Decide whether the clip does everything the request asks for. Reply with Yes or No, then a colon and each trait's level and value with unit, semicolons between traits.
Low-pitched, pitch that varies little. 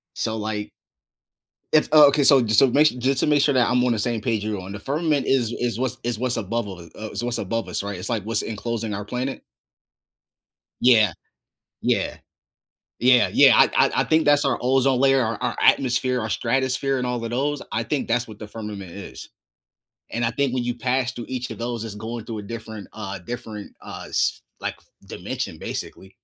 No: low, 120 Hz; average, 3.1 semitones